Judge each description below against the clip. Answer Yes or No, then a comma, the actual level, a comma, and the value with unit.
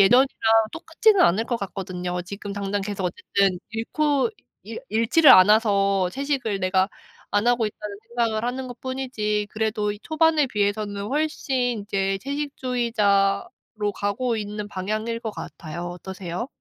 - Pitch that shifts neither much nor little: Yes, average, 3.8 semitones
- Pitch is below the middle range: No, high, 210 Hz